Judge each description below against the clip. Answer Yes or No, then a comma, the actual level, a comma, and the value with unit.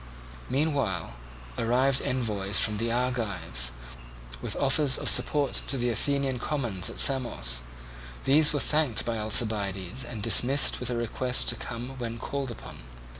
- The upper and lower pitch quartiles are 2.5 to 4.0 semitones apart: Yes, average, 3.7 semitones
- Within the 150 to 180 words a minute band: No, average, 140 wpm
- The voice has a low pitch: Yes, low, 120 Hz